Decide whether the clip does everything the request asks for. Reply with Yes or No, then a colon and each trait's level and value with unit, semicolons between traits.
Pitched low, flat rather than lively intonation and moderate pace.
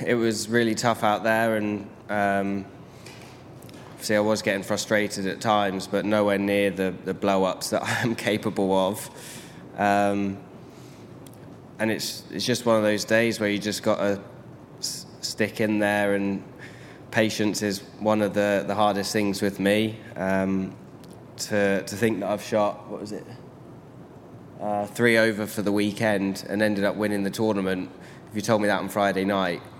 Yes: low, 105 Hz; narrow, 1.7 semitones; average, 170 wpm